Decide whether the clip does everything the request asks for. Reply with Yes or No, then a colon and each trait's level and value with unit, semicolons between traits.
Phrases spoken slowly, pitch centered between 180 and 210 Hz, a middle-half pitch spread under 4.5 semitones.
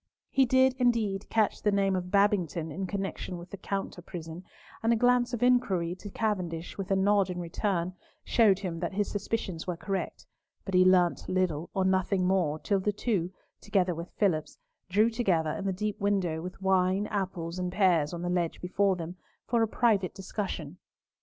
No: average, 185 wpm; high, 190 Hz; narrow, 2.6 semitones